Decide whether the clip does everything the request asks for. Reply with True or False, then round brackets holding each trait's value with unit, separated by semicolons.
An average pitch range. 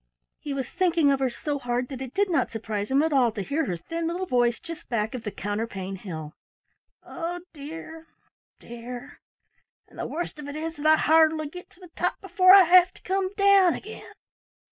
False (6.3 semitones)